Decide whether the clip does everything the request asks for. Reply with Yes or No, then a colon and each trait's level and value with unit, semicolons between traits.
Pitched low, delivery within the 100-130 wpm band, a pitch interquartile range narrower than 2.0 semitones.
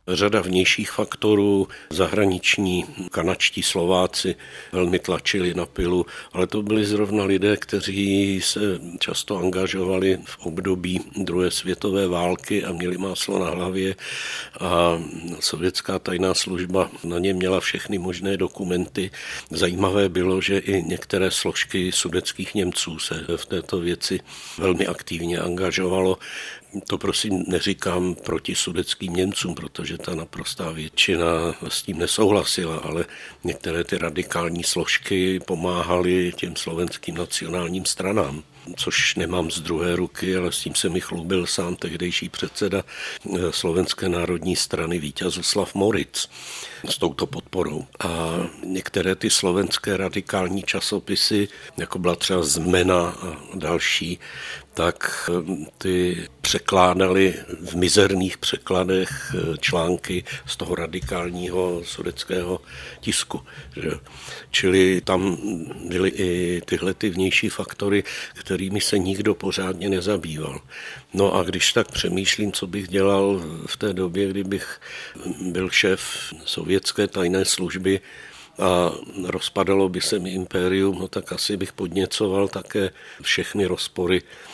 Yes: very low, 95 Hz; average, 120 wpm; narrow, 1.6 semitones